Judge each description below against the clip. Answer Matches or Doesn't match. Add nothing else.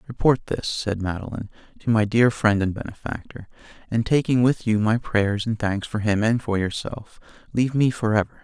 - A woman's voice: Doesn't match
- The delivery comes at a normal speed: Matches